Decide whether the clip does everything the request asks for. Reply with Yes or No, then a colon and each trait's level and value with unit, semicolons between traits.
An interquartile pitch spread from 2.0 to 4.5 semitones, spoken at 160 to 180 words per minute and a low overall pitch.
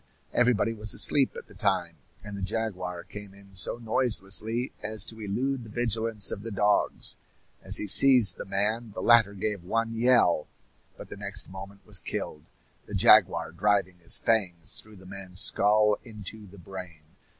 Yes: average, 2.8 semitones; average, 170 wpm; low, 105 Hz